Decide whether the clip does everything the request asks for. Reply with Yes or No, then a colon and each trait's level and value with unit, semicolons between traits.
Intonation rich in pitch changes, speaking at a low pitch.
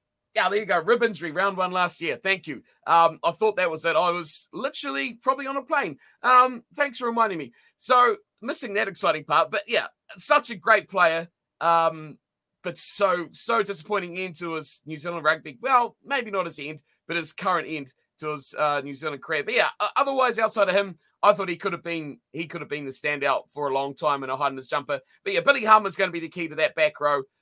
No: wide, 6.6 semitones; medium, 175 Hz